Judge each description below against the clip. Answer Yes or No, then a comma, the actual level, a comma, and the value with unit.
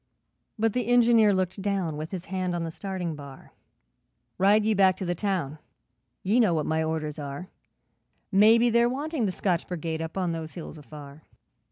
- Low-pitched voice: No, medium, 185 Hz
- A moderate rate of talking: Yes, average, 180 wpm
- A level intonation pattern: No, average, 4.7 semitones